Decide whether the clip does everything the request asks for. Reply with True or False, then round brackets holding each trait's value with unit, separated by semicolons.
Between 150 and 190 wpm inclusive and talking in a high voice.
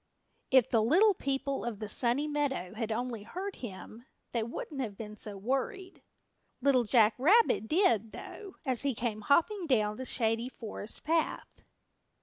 True (155 wpm; 245 Hz)